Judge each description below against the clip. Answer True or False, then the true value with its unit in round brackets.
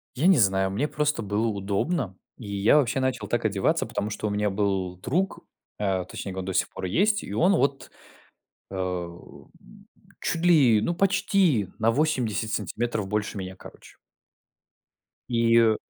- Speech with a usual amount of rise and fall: False (6.2 semitones)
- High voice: False (110 Hz)